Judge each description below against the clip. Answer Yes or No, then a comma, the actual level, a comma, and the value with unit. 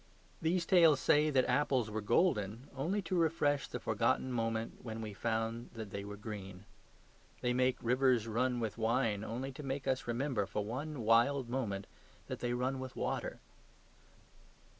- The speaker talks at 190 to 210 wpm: No, average, 160 wpm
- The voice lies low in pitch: Yes, low, 120 Hz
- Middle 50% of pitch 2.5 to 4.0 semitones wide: Yes, average, 3.5 semitones